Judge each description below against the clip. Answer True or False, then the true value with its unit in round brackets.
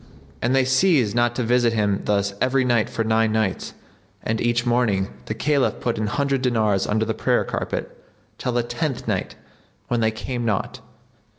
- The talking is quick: False (180 wpm)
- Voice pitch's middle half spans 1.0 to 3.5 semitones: True (2.5 semitones)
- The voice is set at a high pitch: False (120 Hz)